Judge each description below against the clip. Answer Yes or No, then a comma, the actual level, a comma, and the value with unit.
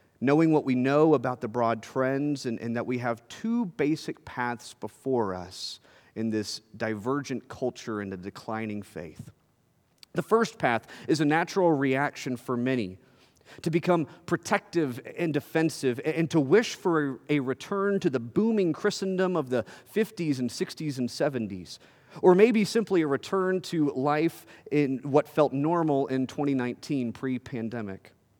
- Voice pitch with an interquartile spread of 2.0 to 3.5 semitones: No, wide, 5.4 semitones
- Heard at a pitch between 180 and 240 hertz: No, medium, 140 Hz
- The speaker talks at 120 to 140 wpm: No, average, 150 wpm